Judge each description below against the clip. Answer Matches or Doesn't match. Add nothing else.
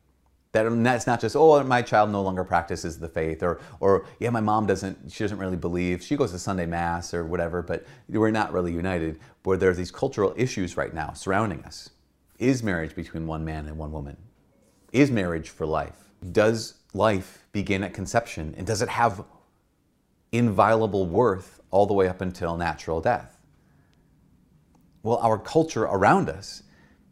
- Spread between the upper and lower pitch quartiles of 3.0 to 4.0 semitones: Doesn't match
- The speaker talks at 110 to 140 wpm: Doesn't match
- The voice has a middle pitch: Doesn't match